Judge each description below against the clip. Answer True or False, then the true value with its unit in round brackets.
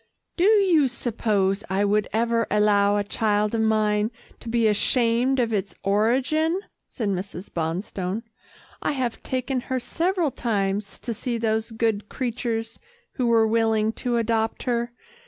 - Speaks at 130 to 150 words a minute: True (145 wpm)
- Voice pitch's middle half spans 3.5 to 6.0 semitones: False (2.8 semitones)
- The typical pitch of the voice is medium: False (225 Hz)